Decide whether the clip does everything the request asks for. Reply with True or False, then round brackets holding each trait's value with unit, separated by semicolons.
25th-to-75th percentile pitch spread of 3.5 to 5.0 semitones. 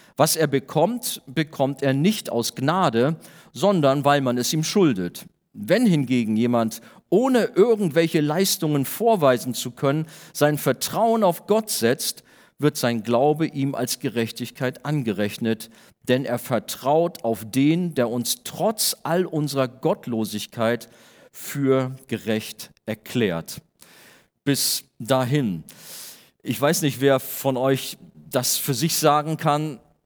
True (4.7 semitones)